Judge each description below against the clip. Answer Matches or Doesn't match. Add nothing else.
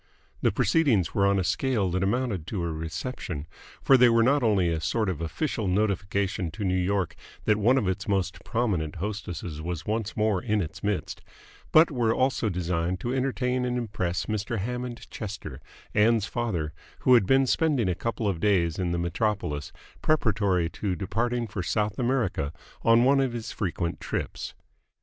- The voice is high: Doesn't match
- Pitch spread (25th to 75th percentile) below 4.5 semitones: Doesn't match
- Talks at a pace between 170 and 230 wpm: Matches